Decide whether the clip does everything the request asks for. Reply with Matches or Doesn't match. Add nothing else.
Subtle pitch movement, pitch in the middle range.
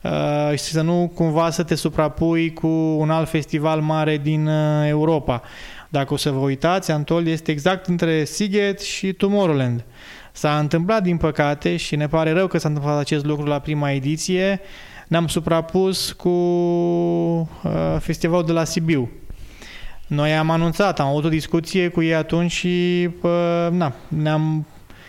Matches